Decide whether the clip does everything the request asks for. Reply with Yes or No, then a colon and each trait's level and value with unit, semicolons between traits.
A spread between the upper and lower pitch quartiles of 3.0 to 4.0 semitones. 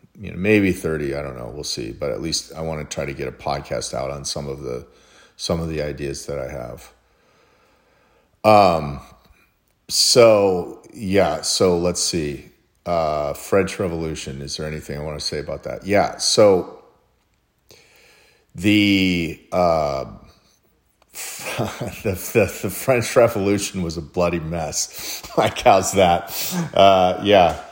No: average, 4.4 semitones